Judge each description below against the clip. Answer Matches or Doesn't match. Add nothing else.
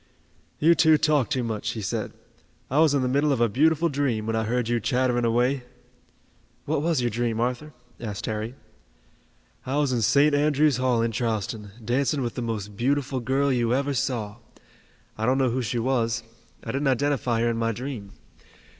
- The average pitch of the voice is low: Matches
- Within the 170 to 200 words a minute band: Matches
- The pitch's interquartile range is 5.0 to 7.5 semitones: Doesn't match